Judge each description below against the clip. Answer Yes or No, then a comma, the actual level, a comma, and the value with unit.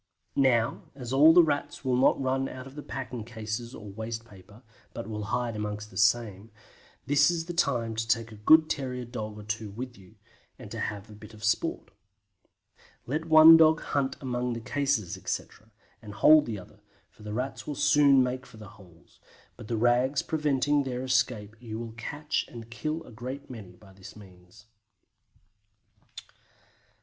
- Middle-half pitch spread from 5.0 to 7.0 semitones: No, average, 4.2 semitones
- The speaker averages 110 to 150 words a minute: No, average, 180 wpm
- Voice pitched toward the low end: Yes, low, 120 Hz